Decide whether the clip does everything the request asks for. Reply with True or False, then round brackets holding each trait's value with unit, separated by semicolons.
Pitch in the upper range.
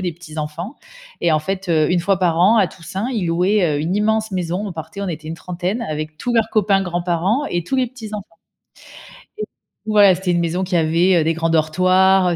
False (180 Hz)